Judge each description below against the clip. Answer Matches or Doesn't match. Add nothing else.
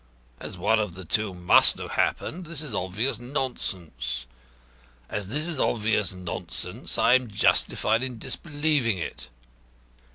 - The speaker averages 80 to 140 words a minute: Matches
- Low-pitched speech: Matches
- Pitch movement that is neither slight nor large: Doesn't match